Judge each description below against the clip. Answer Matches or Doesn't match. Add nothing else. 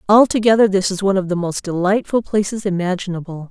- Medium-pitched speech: Doesn't match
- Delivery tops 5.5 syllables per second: Matches